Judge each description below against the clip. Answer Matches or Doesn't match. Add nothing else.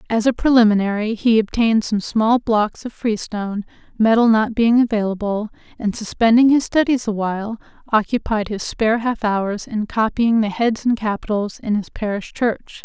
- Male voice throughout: Doesn't match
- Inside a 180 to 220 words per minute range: Doesn't match